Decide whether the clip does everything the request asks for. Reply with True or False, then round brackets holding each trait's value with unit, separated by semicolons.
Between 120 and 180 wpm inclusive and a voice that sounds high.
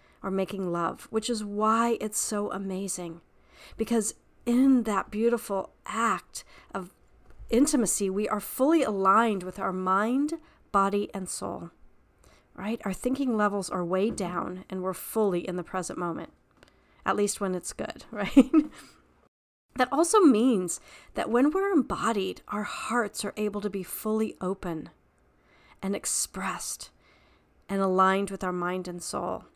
True (140 wpm; 200 Hz)